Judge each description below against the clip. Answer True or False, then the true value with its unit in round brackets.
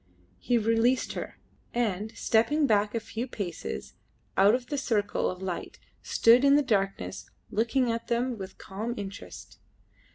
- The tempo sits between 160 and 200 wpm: False (150 wpm)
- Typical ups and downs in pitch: True (3.4 semitones)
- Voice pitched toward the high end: True (225 Hz)